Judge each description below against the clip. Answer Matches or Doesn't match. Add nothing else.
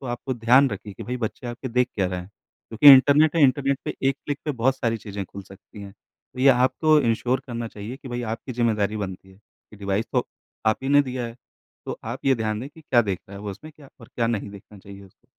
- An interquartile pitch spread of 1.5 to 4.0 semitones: Doesn't match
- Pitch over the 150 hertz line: Doesn't match